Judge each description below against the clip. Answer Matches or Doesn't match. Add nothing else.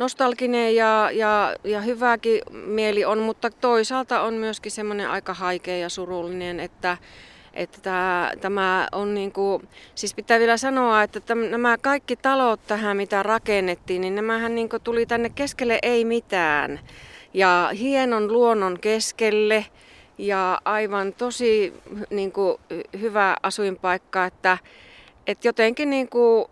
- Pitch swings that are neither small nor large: Matches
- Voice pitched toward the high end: Matches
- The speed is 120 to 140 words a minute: Matches